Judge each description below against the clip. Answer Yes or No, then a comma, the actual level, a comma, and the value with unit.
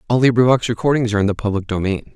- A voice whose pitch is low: Yes, low, 110 Hz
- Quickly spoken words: Yes, fast, 225 wpm